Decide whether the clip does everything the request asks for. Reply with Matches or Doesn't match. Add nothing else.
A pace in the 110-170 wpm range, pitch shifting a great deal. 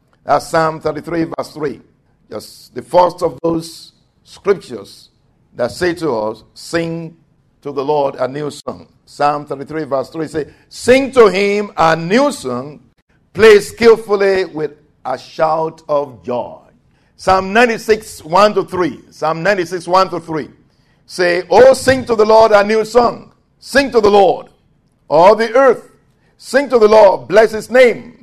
Matches